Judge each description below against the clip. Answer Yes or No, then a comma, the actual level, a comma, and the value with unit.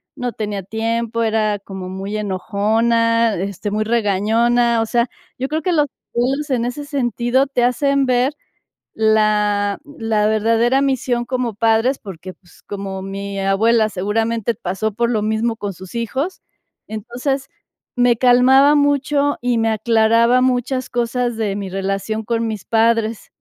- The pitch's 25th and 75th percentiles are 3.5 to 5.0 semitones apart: No, average, 2.8 semitones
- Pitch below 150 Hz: No, high, 230 Hz